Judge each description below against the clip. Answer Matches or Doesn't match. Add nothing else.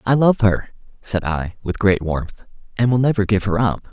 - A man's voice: Matches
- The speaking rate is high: Matches